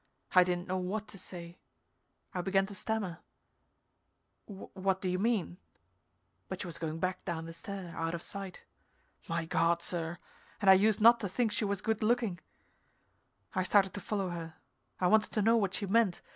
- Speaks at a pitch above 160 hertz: Yes, high, 190 Hz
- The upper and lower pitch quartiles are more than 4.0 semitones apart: No, average, 3.1 semitones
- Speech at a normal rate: Yes, average, 185 wpm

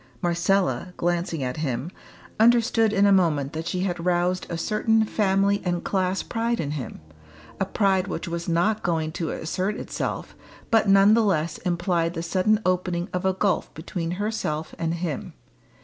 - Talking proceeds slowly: No, average, 165 wpm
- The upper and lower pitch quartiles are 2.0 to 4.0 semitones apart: Yes, average, 2.9 semitones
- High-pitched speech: No, medium, 180 Hz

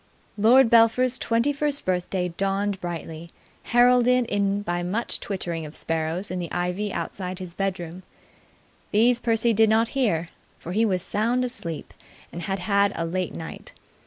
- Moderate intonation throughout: Yes, average, 4.6 semitones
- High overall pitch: Yes, high, 200 Hz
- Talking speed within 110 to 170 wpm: Yes, average, 155 wpm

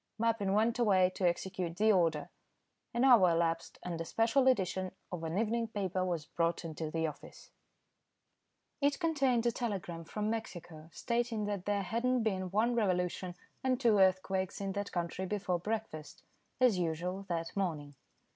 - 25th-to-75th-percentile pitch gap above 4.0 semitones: Yes, average, 4.6 semitones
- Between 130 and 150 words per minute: No, average, 160 wpm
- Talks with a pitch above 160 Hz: Yes, high, 190 Hz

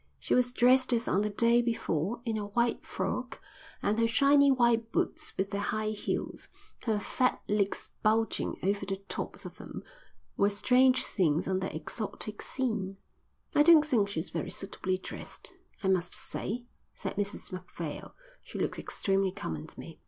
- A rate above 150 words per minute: Yes, average, 165 wpm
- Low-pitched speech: No, high, 210 Hz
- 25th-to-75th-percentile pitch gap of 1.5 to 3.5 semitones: No, average, 3.9 semitones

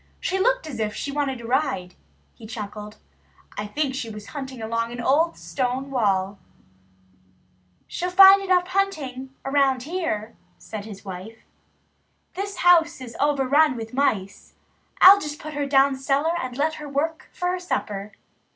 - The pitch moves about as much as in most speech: No, wide, 5.9 semitones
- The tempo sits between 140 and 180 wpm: Yes, average, 150 wpm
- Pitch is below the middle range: No, very high, 270 Hz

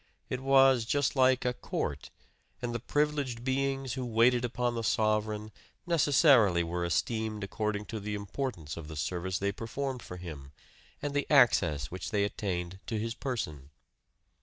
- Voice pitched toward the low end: Yes, low, 115 Hz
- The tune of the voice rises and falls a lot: Yes, wide, 5.8 semitones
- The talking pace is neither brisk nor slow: Yes, average, 160 wpm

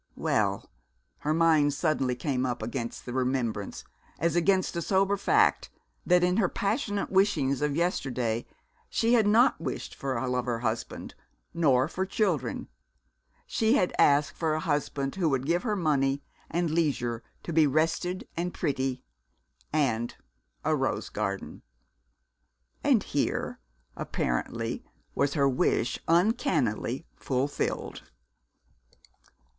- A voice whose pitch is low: No, medium, 150 Hz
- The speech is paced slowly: Yes, slow, 125 wpm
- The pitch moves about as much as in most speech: No, wide, 5.7 semitones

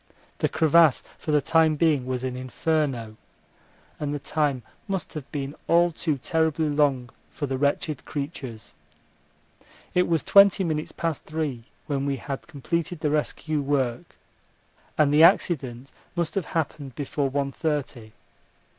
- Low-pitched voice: No, medium, 145 Hz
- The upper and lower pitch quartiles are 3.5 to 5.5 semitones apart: No, average, 3.0 semitones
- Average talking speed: Yes, average, 145 wpm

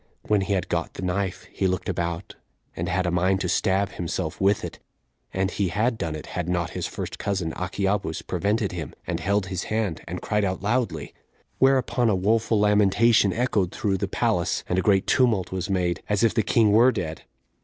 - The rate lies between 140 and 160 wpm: No, average, 200 wpm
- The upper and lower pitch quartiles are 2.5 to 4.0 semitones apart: Yes, average, 2.8 semitones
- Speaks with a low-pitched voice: Yes, very low, 95 Hz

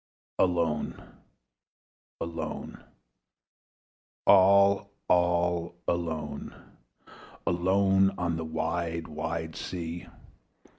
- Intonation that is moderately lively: No, narrow, 1.9 semitones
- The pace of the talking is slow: Yes, slow, 60 wpm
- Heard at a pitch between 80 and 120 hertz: Yes, very low, 85 Hz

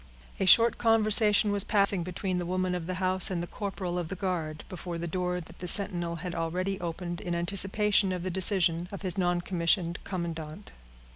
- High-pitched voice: No, medium, 180 Hz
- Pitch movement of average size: No, narrow, 2.1 semitones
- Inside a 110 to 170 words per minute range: No, average, 190 wpm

